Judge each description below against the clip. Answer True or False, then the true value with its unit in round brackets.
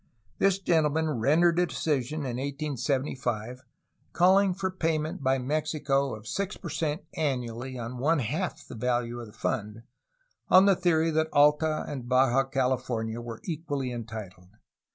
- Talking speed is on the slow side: False (145 wpm)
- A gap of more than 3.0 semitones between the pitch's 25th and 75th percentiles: True (4.6 semitones)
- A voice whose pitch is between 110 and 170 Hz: True (140 Hz)